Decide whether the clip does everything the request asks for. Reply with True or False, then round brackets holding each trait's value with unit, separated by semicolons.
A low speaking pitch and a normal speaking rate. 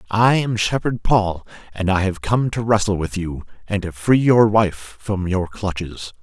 True (100 Hz; 195 wpm)